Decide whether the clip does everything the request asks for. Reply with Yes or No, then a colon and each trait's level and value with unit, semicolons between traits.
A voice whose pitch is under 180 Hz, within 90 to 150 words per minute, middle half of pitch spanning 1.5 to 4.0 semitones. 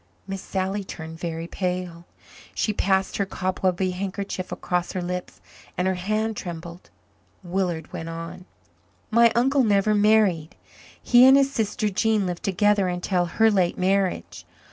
No: high, 190 Hz; average, 145 wpm; average, 2.7 semitones